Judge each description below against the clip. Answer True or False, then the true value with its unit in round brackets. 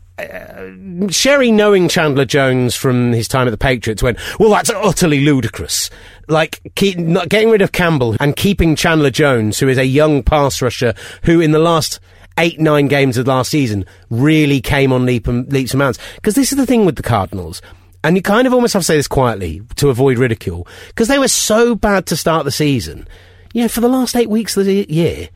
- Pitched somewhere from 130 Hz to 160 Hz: True (140 Hz)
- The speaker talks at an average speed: False (220 wpm)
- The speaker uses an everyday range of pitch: False (7.5 semitones)